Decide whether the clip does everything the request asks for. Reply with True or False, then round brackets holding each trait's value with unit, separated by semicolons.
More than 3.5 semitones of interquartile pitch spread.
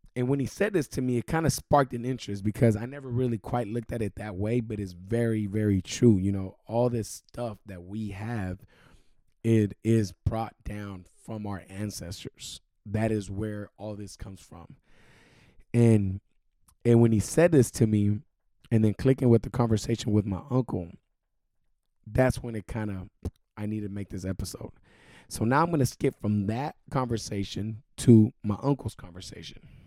False (2.9 semitones)